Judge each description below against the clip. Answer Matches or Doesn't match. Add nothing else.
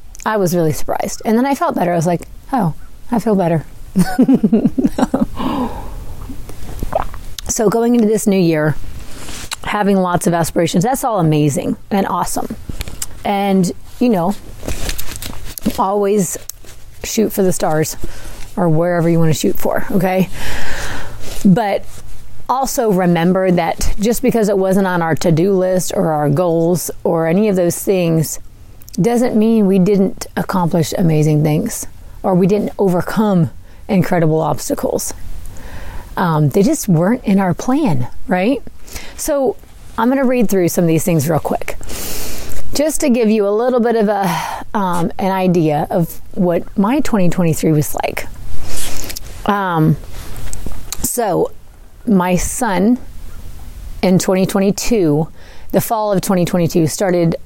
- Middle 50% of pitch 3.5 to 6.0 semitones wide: Matches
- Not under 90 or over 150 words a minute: Matches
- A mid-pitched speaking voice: Matches